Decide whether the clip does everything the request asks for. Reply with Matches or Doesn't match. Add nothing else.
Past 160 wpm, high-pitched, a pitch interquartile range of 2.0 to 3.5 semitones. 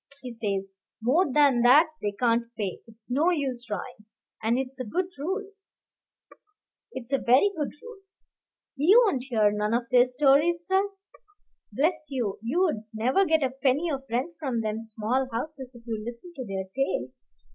Doesn't match